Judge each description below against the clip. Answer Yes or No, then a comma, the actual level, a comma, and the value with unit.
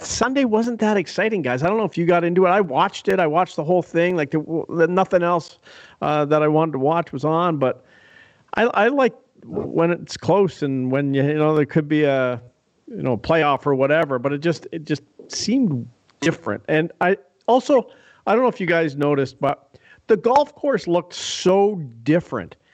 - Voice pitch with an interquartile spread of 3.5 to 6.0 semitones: Yes, average, 4.2 semitones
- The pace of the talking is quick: Yes, fast, 210 wpm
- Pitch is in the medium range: Yes, medium, 165 Hz